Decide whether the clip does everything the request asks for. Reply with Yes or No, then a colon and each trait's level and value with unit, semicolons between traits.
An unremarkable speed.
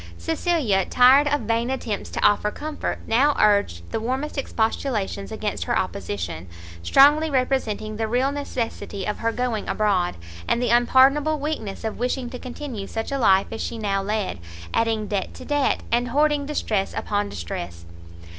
Yes: average, 160 wpm